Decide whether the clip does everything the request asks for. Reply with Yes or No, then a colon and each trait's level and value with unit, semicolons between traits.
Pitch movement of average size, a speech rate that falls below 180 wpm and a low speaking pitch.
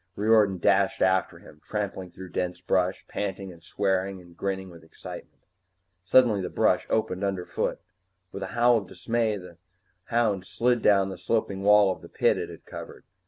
No: narrow, 2.2 semitones; average, 170 wpm; very low, 95 Hz